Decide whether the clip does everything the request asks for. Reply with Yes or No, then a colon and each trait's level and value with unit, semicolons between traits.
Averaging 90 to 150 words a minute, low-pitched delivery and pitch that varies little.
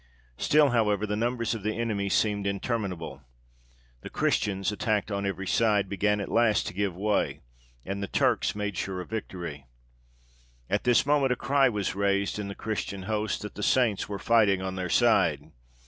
No: average, 180 wpm; low, 105 Hz; narrow, 2.3 semitones